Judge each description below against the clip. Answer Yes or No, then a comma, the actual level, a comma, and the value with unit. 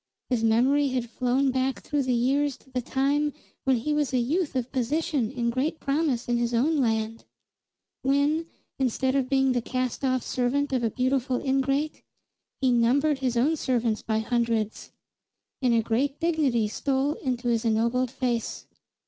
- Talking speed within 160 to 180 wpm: Yes, average, 165 wpm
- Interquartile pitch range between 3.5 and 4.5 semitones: No, average, 2.8 semitones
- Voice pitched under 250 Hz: No, very high, 255 Hz